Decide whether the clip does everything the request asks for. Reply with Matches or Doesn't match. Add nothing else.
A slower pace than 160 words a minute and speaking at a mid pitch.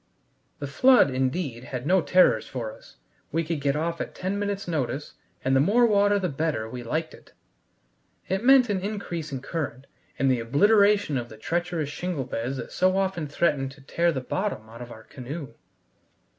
Doesn't match